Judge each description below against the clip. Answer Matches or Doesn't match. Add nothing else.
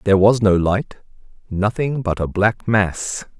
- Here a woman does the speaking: Doesn't match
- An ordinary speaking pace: Matches